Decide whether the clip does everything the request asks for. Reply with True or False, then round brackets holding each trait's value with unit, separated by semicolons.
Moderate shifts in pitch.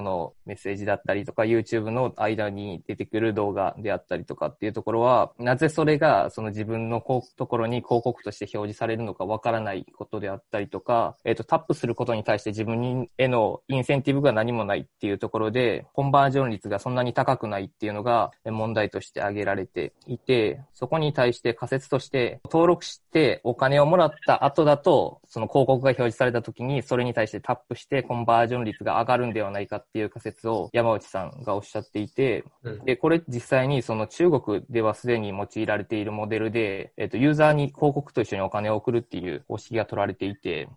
True (3.4 semitones)